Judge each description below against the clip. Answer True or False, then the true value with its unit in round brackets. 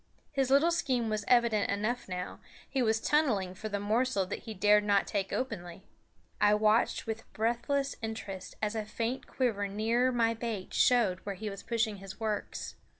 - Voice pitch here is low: False (220 Hz)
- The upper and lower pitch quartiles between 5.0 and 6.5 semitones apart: False (2.9 semitones)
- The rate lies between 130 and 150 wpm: False (175 wpm)